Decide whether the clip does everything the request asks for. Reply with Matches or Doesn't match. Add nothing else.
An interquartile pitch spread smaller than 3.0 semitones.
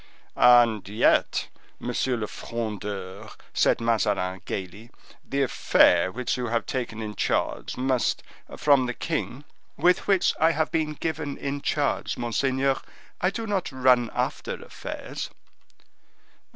Doesn't match